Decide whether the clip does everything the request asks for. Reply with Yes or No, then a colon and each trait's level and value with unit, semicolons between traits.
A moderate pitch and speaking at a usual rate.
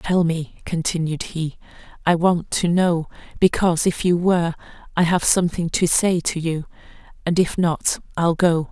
Yes: medium, 170 Hz; average, 145 wpm